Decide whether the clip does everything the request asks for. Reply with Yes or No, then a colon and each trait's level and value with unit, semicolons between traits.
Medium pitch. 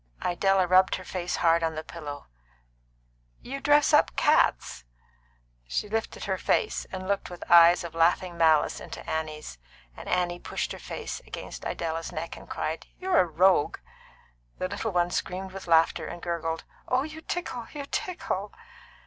Yes: medium, 180 Hz